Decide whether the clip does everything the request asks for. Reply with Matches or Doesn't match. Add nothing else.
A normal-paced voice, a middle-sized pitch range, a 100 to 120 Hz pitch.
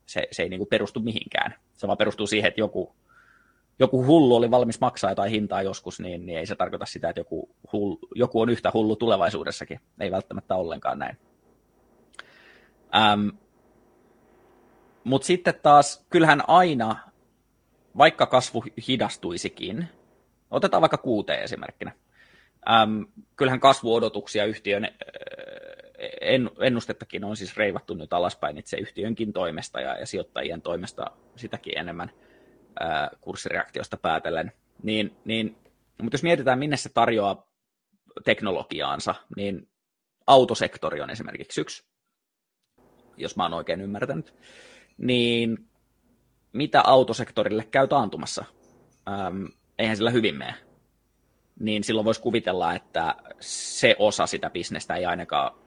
Matches